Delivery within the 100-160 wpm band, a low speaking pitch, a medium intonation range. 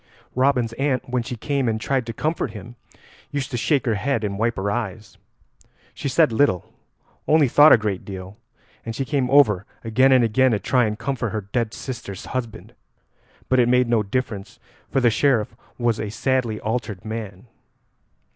No: average, 180 wpm; low, 120 Hz; average, 3.5 semitones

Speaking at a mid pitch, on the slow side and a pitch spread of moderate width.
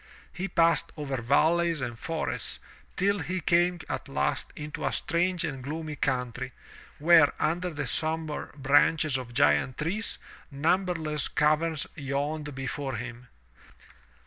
Yes: medium, 150 Hz; slow, 125 wpm; average, 3.7 semitones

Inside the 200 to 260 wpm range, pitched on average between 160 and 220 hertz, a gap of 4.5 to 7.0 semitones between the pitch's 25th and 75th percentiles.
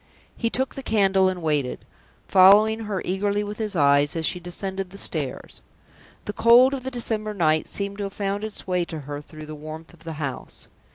Yes: fast, 205 wpm; high, 190 Hz; average, 4.9 semitones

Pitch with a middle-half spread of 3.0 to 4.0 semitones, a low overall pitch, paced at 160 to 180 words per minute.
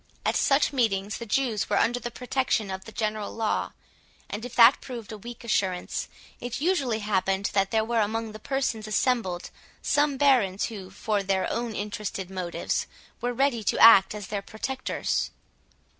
No: average, 3.4 semitones; high, 220 Hz; average, 170 wpm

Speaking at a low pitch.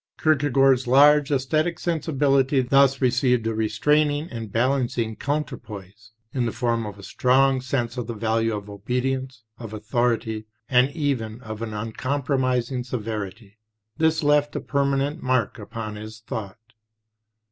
Yes: low, 125 Hz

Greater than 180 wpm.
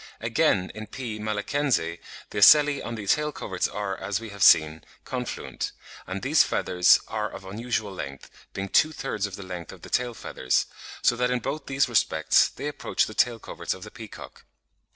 Yes: average, 190 wpm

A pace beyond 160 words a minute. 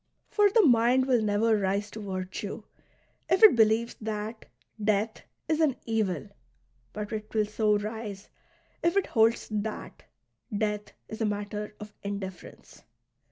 No: average, 140 wpm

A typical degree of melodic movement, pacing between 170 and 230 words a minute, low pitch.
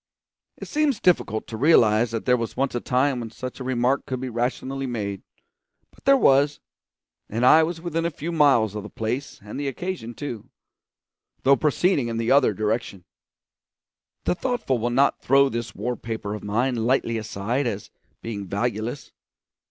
Yes: average, 3.9 semitones; average, 175 wpm; low, 125 Hz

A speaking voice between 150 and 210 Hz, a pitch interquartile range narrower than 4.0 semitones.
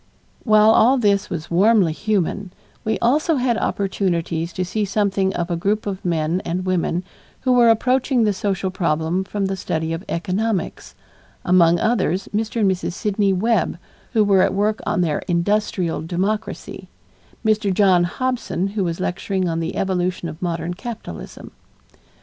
Yes: high, 190 Hz; average, 3.5 semitones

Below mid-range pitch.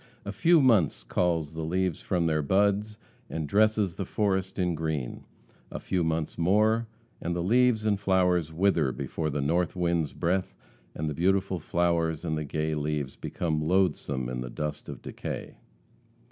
Yes: very low, 85 Hz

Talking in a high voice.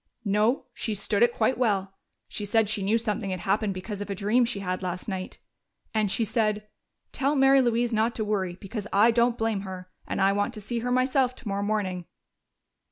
Yes: high, 210 Hz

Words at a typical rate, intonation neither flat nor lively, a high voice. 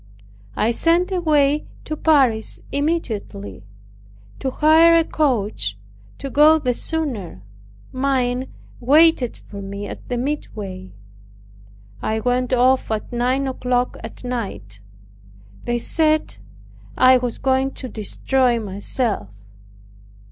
No: slow, 110 wpm; average, 5.0 semitones; very high, 250 Hz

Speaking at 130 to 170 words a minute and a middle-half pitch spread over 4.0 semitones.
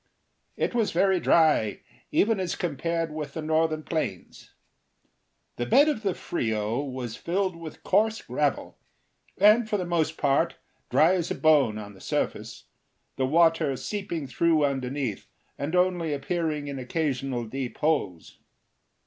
Yes: average, 140 wpm; average, 4.4 semitones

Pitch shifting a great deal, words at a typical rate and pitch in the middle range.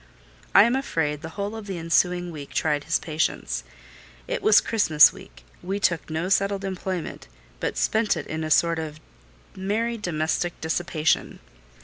No: average, 3.9 semitones; average, 160 wpm; medium, 175 Hz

